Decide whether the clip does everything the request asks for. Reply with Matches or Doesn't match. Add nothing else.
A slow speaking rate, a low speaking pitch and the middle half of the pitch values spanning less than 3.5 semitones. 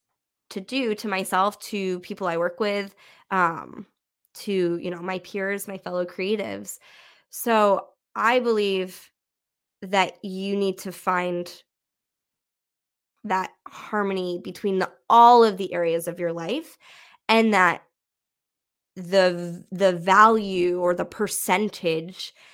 Doesn't match